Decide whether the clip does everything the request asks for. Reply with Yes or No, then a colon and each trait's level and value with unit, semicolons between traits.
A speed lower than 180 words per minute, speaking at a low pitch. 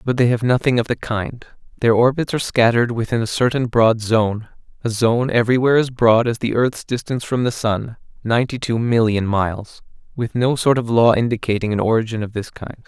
No: average, 190 wpm; low, 115 Hz